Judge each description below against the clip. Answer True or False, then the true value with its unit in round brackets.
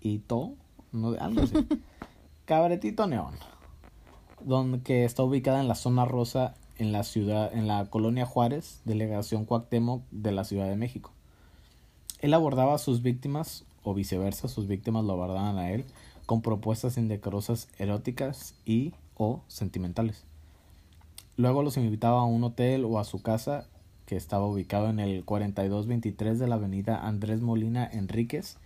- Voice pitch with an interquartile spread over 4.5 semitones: False (3.6 semitones)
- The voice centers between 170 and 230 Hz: False (110 Hz)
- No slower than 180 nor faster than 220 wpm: False (145 wpm)